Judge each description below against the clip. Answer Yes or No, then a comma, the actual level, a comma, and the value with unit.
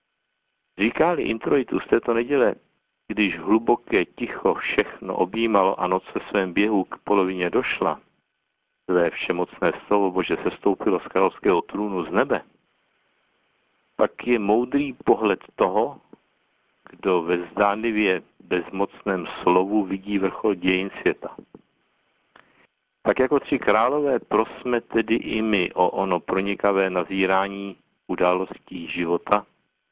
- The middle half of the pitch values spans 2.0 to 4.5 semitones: Yes, average, 3.0 semitones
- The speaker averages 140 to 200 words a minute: No, slow, 115 wpm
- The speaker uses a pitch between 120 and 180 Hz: No, low, 100 Hz